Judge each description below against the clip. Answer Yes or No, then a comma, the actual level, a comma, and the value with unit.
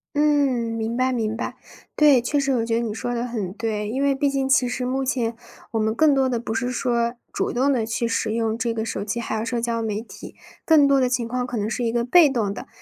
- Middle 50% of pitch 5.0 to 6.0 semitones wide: No, average, 2.7 semitones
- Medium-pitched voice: No, high, 235 Hz